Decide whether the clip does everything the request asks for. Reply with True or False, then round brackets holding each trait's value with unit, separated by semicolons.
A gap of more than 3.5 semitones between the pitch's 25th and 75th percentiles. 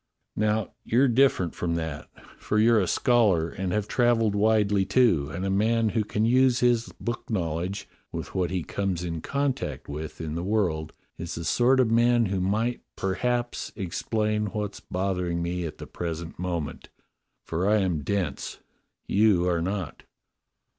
True (4.7 semitones)